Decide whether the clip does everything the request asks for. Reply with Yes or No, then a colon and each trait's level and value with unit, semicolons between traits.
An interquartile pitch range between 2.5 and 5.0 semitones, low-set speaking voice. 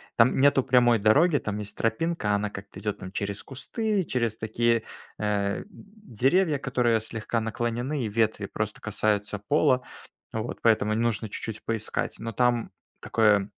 Yes: average, 3.3 semitones; low, 115 Hz